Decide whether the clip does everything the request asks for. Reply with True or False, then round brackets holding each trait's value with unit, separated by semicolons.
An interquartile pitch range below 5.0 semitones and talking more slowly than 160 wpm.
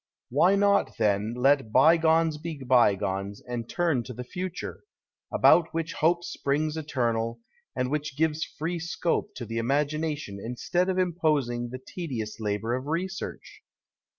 False (5.6 semitones; 140 wpm)